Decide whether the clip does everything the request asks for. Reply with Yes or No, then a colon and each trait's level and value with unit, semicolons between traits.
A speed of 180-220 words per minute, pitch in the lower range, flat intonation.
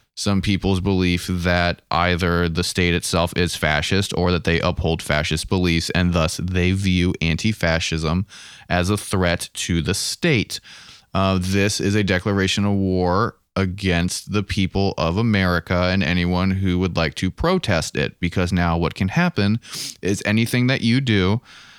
No: average, 160 wpm; very low, 90 Hz; narrow, 2.2 semitones